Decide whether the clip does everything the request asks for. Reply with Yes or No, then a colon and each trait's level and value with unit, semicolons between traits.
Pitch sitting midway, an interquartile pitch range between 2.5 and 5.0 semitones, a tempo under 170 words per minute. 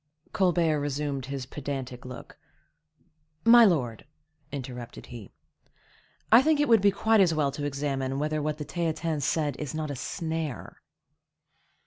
Yes: medium, 150 Hz; average, 3.7 semitones; average, 140 wpm